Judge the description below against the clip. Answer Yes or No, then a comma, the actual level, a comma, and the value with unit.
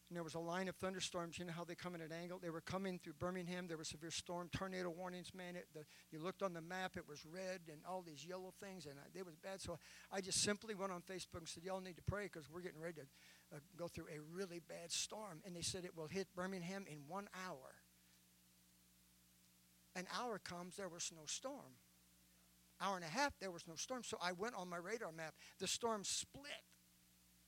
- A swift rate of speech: Yes, fast, 235 wpm